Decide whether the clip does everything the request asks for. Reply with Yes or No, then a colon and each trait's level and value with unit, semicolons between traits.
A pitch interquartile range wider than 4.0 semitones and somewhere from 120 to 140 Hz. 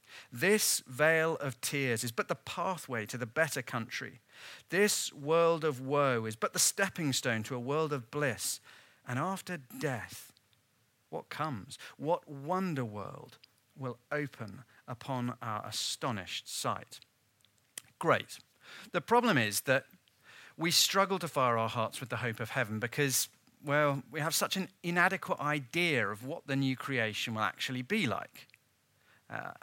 Yes: wide, 5.4 semitones; low, 135 Hz